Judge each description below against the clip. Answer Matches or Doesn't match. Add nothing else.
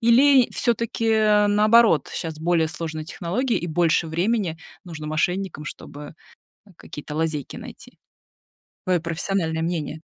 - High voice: Doesn't match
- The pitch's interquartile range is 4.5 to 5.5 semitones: Matches